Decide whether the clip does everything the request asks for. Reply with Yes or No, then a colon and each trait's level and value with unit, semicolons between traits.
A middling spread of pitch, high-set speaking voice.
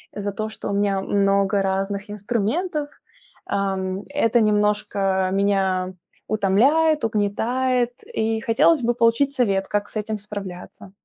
Yes: average, 3.0 semitones; high, 205 Hz